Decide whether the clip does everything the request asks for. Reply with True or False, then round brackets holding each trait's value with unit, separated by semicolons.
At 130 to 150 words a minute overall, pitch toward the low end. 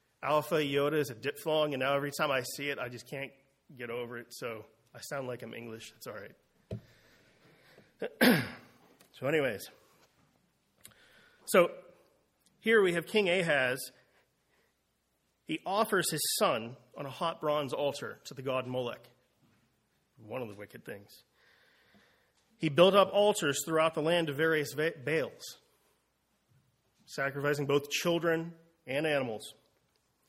False (135 wpm; 145 Hz)